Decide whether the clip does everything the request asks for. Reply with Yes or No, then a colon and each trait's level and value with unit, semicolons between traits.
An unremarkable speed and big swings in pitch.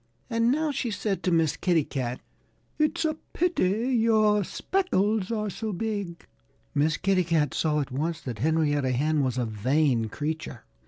Yes: average, 160 wpm; wide, 7.1 semitones